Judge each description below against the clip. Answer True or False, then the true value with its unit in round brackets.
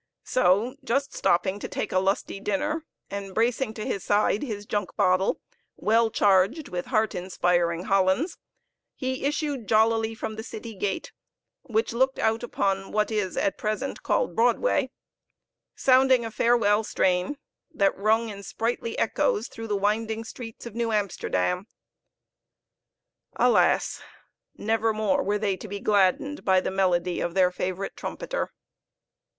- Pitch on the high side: True (215 Hz)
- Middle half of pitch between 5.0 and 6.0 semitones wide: False (3.4 semitones)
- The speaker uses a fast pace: False (145 wpm)